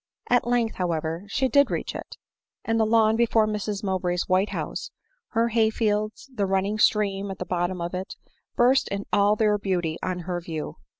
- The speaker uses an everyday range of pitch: Yes, average, 3.4 semitones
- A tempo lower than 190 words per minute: No, average, 195 wpm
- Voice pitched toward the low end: No, high, 205 Hz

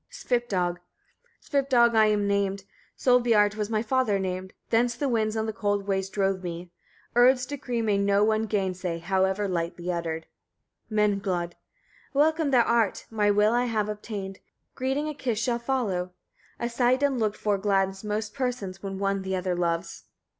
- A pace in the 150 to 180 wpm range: Yes, average, 165 wpm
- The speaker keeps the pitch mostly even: No, average, 3.7 semitones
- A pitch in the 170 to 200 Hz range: No, high, 210 Hz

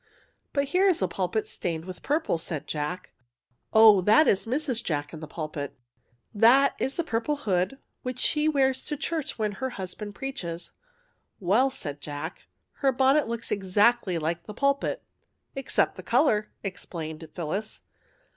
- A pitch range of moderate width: No, wide, 7.7 semitones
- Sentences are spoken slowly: No, average, 175 wpm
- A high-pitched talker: Yes, high, 215 Hz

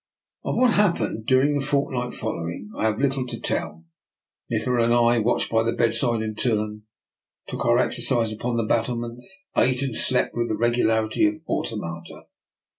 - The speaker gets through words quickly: No, average, 170 wpm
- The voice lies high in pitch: No, low, 120 Hz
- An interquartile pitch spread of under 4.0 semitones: Yes, narrow, 2.6 semitones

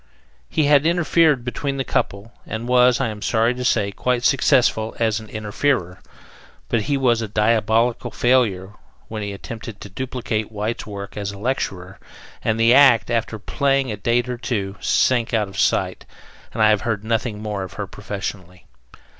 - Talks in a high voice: No, low, 115 Hz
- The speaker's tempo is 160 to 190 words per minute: Yes, average, 170 wpm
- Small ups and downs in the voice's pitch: No, average, 3.3 semitones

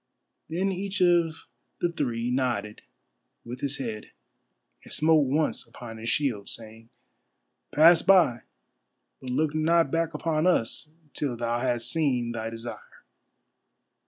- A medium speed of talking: No, slow, 130 wpm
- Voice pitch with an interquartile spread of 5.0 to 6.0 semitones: Yes, wide, 5.6 semitones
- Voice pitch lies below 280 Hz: Yes, low, 135 Hz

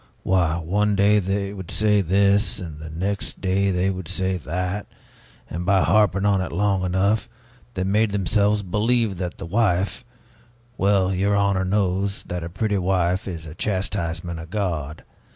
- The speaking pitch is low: Yes, very low, 95 Hz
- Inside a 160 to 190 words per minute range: Yes, average, 165 wpm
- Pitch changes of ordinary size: No, narrow, 2.3 semitones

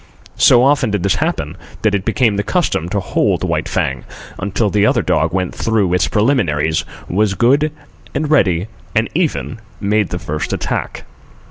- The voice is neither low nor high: No, low, 105 Hz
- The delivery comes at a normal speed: Yes, average, 165 wpm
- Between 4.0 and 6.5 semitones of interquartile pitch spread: Yes, average, 4.7 semitones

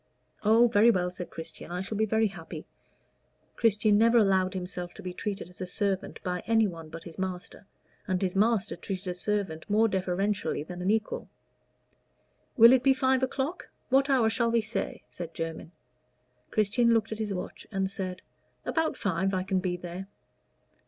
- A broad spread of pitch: No, average, 3.6 semitones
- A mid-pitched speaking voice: No, high, 195 Hz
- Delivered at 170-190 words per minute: Yes, average, 175 wpm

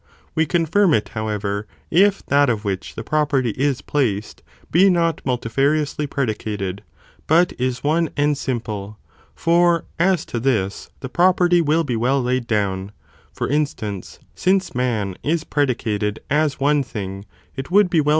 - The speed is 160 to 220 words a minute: No, average, 150 wpm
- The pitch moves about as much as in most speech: No, wide, 6.7 semitones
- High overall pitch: No, low, 135 Hz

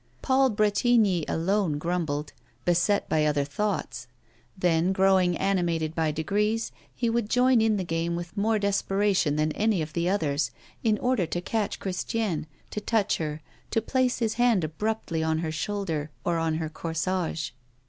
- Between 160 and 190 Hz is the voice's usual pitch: Yes, medium, 185 Hz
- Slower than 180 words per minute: Yes, average, 160 wpm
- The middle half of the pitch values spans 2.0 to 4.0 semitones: No, average, 4.8 semitones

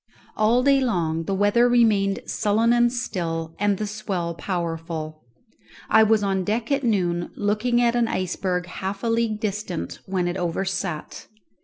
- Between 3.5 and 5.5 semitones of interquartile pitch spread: Yes, average, 4.5 semitones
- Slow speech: No, average, 155 wpm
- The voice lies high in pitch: Yes, high, 200 Hz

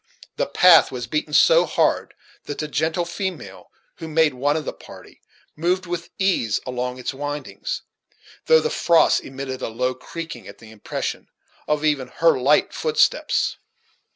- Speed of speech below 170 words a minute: Yes, average, 155 wpm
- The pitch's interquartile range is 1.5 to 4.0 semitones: No, average, 4.8 semitones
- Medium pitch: Yes, medium, 150 Hz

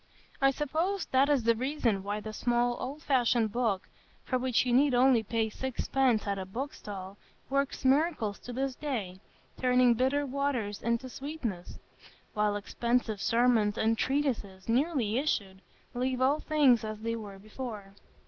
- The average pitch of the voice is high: Yes, high, 245 Hz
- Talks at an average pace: Yes, average, 155 wpm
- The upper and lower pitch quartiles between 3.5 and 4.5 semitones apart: Yes, average, 3.9 semitones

